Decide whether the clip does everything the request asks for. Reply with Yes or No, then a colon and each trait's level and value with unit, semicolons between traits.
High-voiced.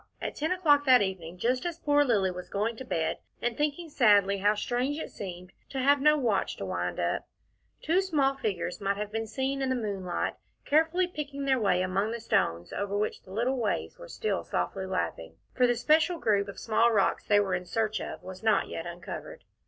Yes: high, 225 Hz